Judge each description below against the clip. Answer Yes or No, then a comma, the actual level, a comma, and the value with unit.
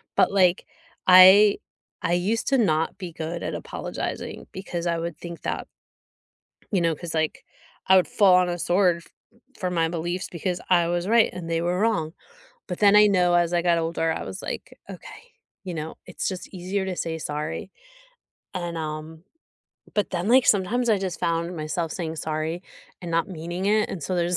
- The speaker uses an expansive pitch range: No, narrow, 2.4 semitones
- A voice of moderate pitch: Yes, medium, 175 Hz